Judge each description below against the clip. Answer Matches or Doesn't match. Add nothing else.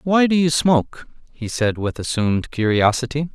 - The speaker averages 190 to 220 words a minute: Doesn't match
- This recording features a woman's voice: Doesn't match